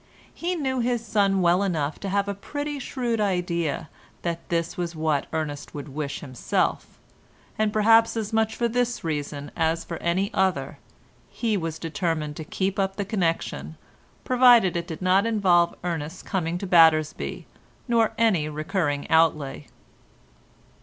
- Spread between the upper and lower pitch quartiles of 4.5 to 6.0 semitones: Yes, average, 5.2 semitones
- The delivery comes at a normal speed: Yes, average, 150 wpm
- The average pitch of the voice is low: No, medium, 175 Hz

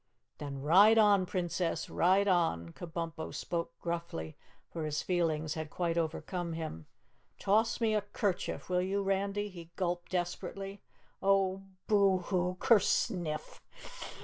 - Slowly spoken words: Yes, slow, 125 wpm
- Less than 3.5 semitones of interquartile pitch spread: Yes, average, 3.1 semitones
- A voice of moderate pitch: Yes, medium, 180 Hz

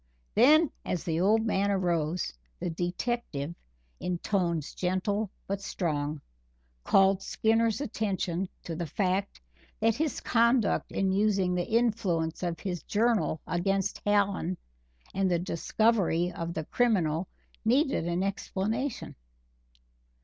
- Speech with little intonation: No, average, 4.1 semitones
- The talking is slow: Yes, slow, 120 wpm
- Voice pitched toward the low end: No, high, 190 Hz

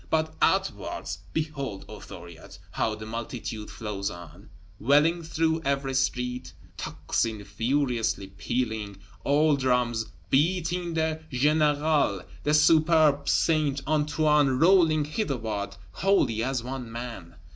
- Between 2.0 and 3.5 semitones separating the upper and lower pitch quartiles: No, wide, 5.6 semitones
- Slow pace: Yes, slow, 110 wpm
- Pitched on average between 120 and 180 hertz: Yes, low, 135 Hz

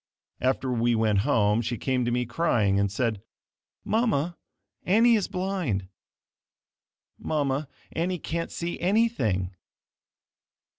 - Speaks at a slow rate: Yes, slow, 110 wpm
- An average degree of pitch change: No, wide, 8.0 semitones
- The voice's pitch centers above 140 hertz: No, low, 130 Hz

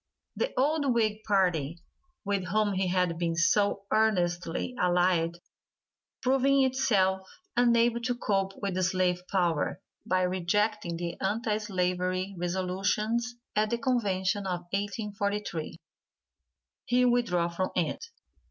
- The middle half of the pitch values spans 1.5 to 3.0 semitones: No, average, 3.6 semitones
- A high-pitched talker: Yes, high, 195 Hz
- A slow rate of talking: Yes, slow, 115 wpm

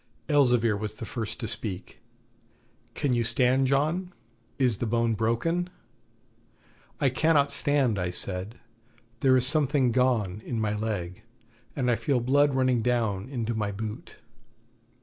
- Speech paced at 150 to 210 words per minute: No, average, 140 wpm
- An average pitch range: Yes, average, 3.6 semitones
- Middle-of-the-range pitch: No, low, 120 Hz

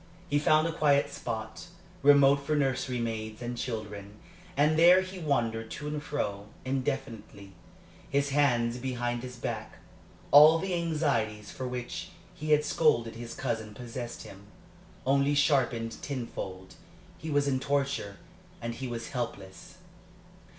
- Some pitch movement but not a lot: Yes, average, 4.2 semitones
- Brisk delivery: No, slow, 135 wpm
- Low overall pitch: Yes, low, 125 Hz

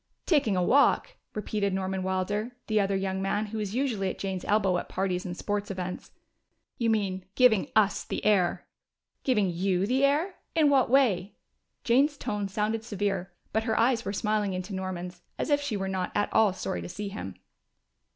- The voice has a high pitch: Yes, high, 205 Hz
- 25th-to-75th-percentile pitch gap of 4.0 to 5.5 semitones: No, average, 3.1 semitones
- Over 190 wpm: No, average, 185 wpm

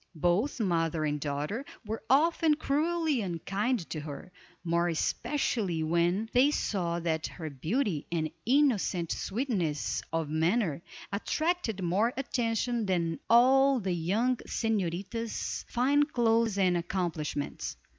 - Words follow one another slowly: Yes, slow, 115 wpm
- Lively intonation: Yes, wide, 6.6 semitones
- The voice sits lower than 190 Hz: No, high, 195 Hz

